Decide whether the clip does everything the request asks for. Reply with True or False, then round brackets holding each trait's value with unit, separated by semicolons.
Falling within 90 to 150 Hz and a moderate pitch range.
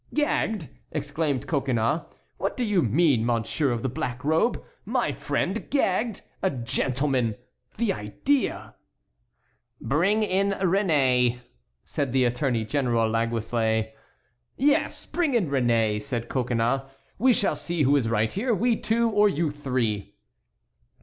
False (140 Hz; 8.6 semitones)